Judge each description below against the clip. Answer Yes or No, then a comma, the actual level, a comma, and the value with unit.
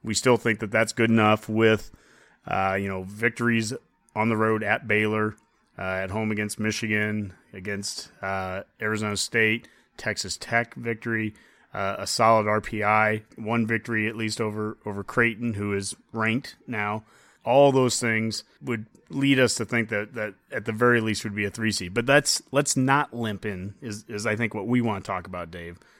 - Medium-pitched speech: No, low, 110 Hz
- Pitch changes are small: Yes, narrow, 1.9 semitones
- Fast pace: No, average, 185 wpm